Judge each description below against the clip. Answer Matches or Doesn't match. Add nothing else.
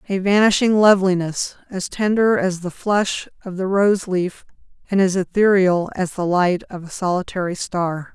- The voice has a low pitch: Doesn't match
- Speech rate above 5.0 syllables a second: Doesn't match